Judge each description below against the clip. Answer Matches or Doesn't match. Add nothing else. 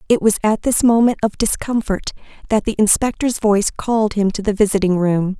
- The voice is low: Doesn't match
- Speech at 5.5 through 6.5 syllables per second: Matches